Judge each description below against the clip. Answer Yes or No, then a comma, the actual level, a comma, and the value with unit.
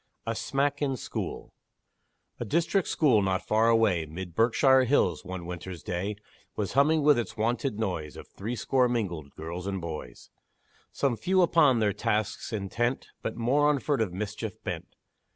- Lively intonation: Yes, wide, 6.2 semitones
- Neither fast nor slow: Yes, average, 155 wpm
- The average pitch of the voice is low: Yes, low, 110 Hz